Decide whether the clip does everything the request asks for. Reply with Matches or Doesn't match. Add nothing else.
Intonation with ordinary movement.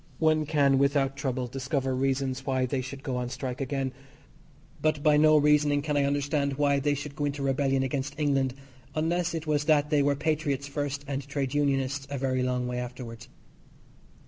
Doesn't match